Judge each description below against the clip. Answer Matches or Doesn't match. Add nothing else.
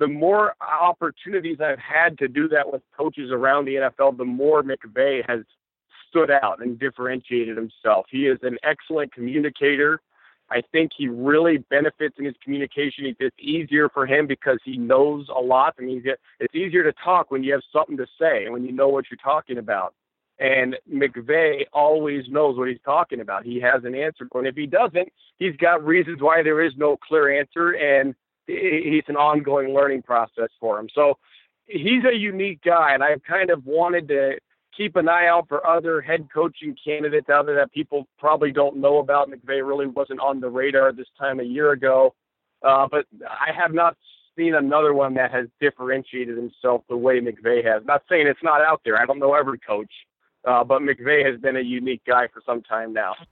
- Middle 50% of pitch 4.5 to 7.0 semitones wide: Doesn't match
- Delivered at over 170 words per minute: Matches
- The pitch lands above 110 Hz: Matches